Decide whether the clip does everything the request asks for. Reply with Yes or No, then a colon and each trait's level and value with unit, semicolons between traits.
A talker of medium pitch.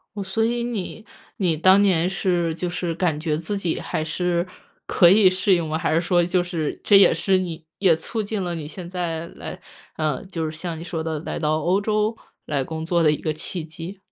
Yes: medium, 175 Hz